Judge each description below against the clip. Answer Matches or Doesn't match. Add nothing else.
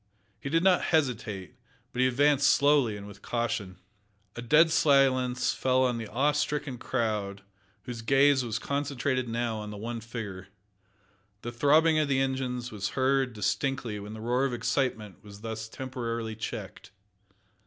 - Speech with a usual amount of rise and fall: Matches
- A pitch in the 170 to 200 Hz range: Doesn't match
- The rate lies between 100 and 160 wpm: Matches